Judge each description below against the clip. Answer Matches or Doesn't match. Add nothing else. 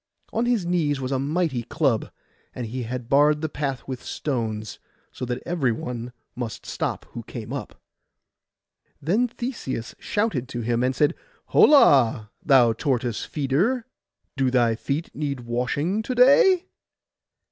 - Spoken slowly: Doesn't match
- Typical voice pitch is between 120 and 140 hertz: Matches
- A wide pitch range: Matches